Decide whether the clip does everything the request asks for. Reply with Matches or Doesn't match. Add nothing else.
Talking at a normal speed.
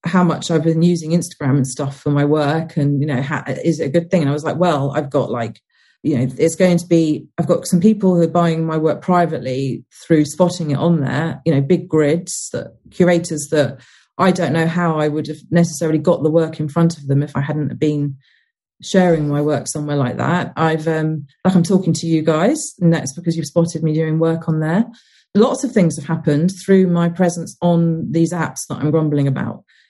Doesn't match